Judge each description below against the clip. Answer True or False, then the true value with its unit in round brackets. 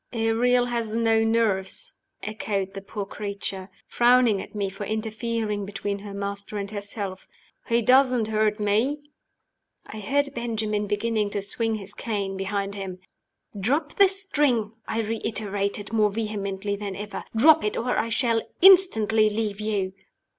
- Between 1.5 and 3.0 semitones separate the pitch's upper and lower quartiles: True (2.4 semitones)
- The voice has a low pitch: False (215 Hz)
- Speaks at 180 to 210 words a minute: False (145 wpm)